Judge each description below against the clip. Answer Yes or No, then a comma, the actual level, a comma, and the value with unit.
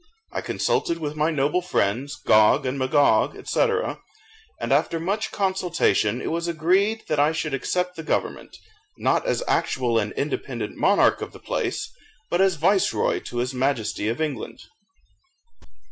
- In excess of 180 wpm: No, average, 150 wpm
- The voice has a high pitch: No, medium, 155 Hz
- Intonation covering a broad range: Yes, wide, 5.7 semitones